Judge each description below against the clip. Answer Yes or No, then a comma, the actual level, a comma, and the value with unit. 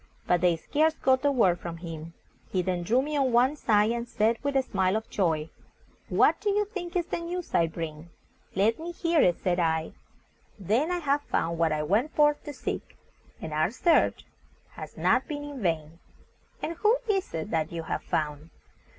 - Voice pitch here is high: Yes, high, 220 Hz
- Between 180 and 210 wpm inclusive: Yes, average, 200 wpm